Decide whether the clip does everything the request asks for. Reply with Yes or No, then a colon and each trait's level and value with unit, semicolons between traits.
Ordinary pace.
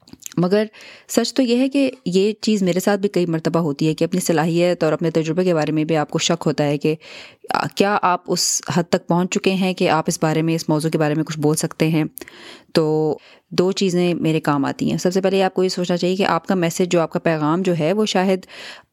No: fast, 255 wpm